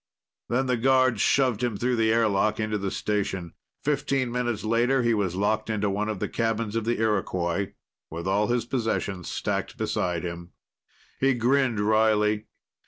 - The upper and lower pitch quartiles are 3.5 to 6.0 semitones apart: No, average, 3.0 semitones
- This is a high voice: No, low, 110 Hz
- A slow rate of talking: No, average, 165 wpm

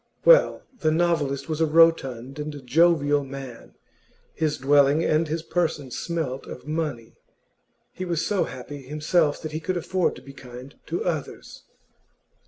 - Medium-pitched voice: Yes, medium, 150 Hz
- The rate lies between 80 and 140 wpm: No, average, 150 wpm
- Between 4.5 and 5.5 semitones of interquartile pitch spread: No, average, 3.2 semitones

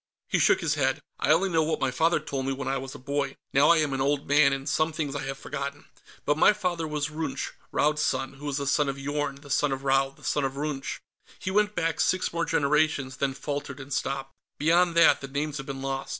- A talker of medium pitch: Yes, medium, 145 Hz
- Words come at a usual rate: No, fast, 250 wpm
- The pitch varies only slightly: Yes, narrow, 2.2 semitones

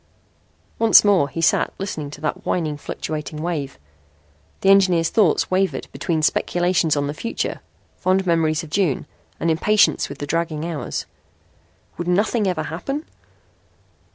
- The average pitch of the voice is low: No, medium, 170 Hz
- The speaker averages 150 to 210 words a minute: No, average, 140 wpm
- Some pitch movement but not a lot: Yes, average, 3.8 semitones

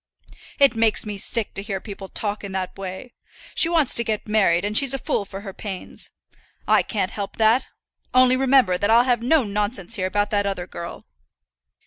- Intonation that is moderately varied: Yes, average, 3.5 semitones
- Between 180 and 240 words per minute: Yes, average, 195 wpm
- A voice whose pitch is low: No, high, 210 Hz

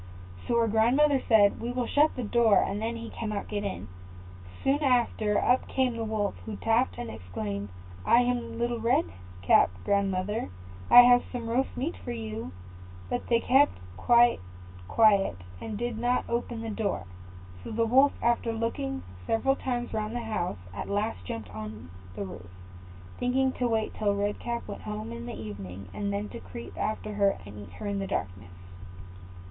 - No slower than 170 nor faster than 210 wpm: Yes, average, 180 wpm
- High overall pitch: Yes, high, 220 Hz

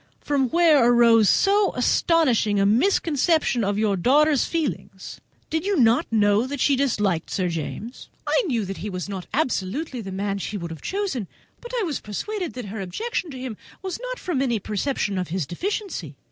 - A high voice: Yes, high, 240 Hz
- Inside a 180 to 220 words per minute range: Yes, average, 190 wpm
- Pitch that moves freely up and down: Yes, wide, 7.9 semitones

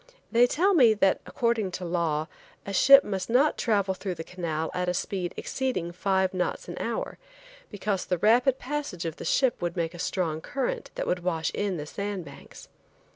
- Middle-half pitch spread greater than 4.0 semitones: Yes, average, 5.2 semitones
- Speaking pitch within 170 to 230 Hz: Yes, high, 190 Hz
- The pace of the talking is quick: No, average, 190 wpm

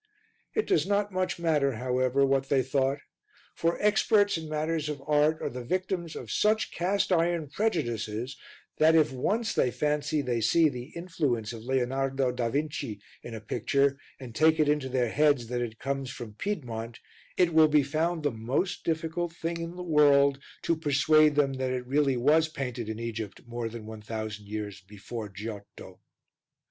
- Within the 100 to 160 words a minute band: No, average, 175 wpm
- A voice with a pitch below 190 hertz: Yes, medium, 140 Hz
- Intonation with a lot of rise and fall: No, average, 5.0 semitones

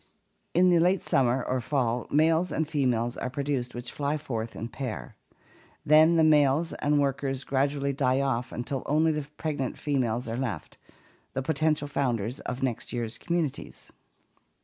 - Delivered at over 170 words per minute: No, average, 160 wpm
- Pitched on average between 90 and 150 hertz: Yes, medium, 140 Hz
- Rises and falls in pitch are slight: No, average, 3.5 semitones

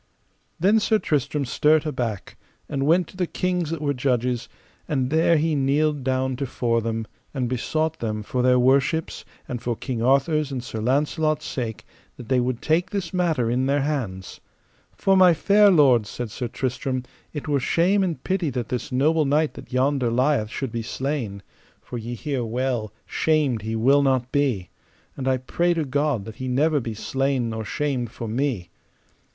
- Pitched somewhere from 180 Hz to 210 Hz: No, low, 135 Hz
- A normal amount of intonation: Yes, average, 4.0 semitones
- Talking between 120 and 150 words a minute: No, average, 180 wpm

